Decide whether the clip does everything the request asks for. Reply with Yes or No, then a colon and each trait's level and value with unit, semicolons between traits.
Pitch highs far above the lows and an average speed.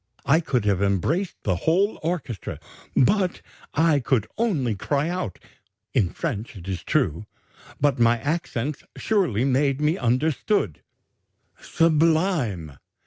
No: wide, 7.5 semitones; slow, 120 wpm